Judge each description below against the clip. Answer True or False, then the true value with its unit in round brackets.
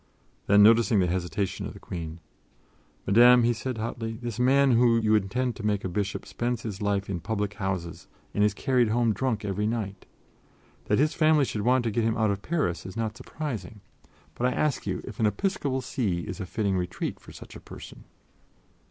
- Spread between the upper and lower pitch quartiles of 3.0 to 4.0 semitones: True (3.6 semitones)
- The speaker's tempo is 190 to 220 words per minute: True (200 wpm)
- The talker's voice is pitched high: False (110 Hz)